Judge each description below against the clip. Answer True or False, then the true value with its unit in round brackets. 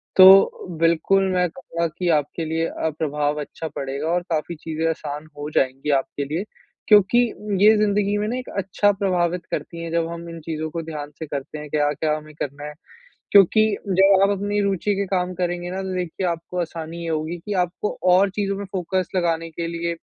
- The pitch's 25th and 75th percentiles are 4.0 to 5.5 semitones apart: False (3.4 semitones)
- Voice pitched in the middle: True (170 Hz)